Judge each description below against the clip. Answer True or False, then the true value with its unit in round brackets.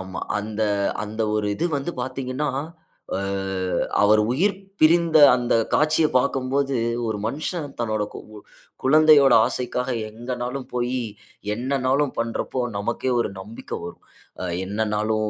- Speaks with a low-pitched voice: True (125 Hz)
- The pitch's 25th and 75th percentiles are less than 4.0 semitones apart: False (4.3 semitones)